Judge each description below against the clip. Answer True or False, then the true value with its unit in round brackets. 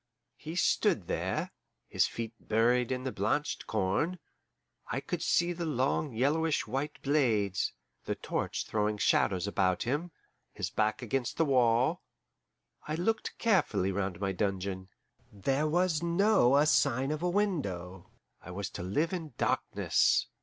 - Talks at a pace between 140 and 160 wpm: True (145 wpm)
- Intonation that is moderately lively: False (7.4 semitones)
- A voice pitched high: False (130 Hz)